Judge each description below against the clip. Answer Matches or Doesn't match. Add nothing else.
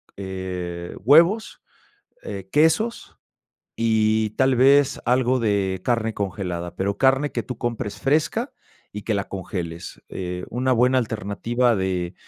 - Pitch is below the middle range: Matches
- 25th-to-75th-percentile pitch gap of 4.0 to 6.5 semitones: Matches